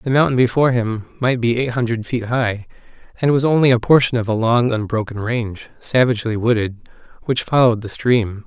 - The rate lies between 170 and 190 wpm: Yes, average, 185 wpm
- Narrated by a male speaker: Yes, male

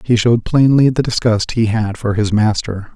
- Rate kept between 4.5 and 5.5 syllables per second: Yes, 4.9 syllables/s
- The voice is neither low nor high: No, low, 115 Hz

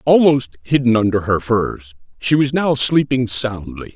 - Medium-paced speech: Yes, average, 150 wpm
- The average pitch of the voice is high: No, low, 125 Hz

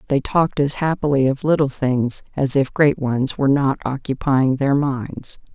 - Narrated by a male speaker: No, female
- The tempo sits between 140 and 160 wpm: No, average, 175 wpm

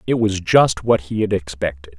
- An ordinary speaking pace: No, fast, 210 wpm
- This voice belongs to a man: Yes, male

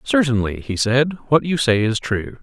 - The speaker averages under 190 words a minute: No, average, 200 wpm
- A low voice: Yes, low, 125 Hz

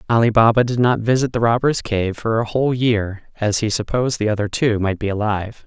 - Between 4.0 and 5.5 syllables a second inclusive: No, 5.8 syllables/s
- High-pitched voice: No, low, 110 Hz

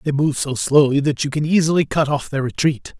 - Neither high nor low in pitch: Yes, medium, 145 Hz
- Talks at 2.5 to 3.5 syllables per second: No, 5.6 syllables/s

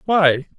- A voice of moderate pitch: Yes, medium, 170 Hz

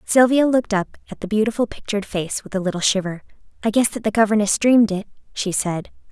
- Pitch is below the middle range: No, high, 210 Hz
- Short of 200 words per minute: No, fast, 205 wpm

